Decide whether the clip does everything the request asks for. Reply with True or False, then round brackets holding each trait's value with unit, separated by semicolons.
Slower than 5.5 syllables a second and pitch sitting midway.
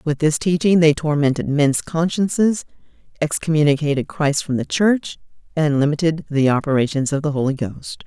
True (5.1 syllables/s; 150 Hz)